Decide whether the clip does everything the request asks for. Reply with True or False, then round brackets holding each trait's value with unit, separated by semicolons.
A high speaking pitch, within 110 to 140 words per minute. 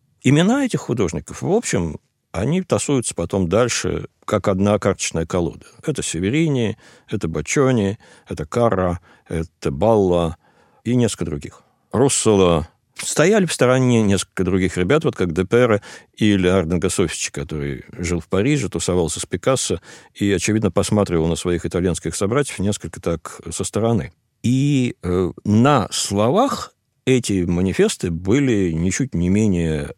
False (100 Hz; 130 wpm)